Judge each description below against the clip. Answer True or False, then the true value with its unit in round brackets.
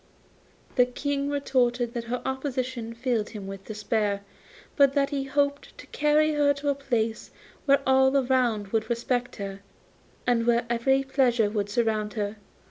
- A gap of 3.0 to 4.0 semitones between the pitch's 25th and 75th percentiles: True (3.7 semitones)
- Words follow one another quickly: False (155 wpm)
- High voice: True (245 Hz)